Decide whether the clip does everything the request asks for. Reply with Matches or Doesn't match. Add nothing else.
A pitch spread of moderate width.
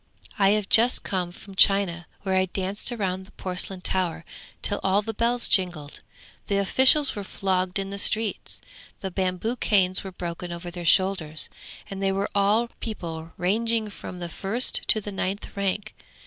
Doesn't match